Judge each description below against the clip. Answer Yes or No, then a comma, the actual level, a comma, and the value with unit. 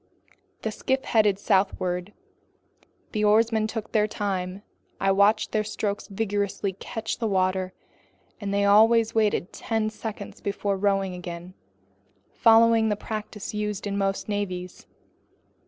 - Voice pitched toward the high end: Yes, high, 205 Hz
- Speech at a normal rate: No, slow, 125 wpm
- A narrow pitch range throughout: Yes, narrow, 1.9 semitones